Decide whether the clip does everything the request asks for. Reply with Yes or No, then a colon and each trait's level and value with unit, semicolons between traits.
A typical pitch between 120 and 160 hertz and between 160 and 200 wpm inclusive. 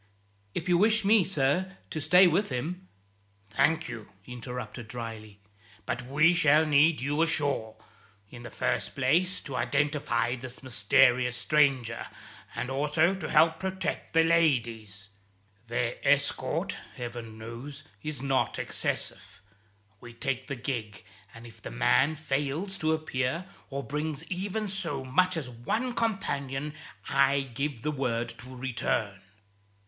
No: low, 135 Hz; average, 140 wpm